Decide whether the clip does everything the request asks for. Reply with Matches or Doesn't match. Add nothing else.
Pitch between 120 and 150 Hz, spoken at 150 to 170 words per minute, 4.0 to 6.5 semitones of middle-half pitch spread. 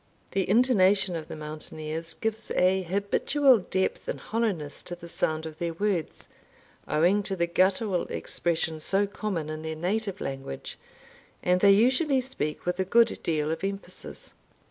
Doesn't match